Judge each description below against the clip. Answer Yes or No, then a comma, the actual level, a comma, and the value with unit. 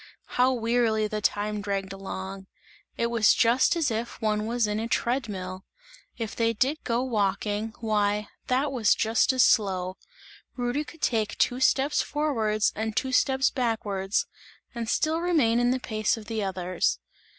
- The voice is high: Yes, high, 225 Hz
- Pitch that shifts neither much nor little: Yes, average, 3.3 semitones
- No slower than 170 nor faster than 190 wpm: No, average, 160 wpm